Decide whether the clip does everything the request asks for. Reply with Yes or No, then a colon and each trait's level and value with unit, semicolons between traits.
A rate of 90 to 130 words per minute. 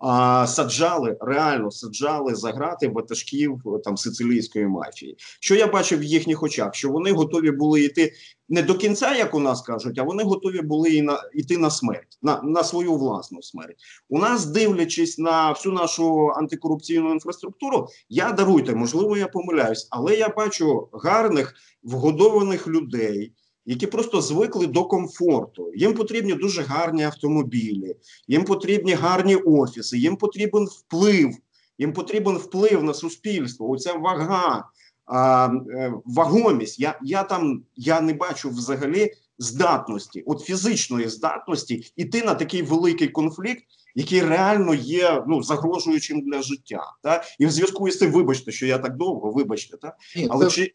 No: average, 145 wpm